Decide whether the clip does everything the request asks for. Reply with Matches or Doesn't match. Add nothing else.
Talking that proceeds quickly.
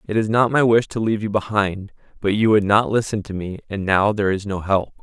Matches